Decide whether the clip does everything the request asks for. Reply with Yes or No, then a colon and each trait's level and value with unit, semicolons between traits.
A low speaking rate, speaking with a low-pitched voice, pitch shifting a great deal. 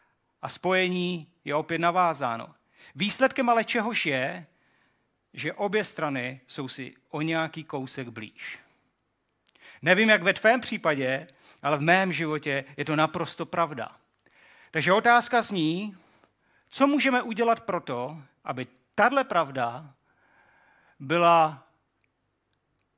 No: slow, 110 wpm; medium, 165 Hz; wide, 5.8 semitones